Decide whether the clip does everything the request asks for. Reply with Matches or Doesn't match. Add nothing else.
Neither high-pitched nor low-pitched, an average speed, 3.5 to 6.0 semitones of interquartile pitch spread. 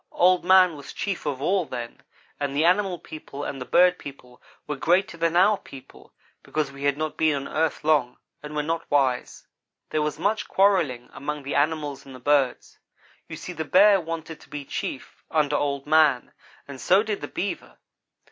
Matches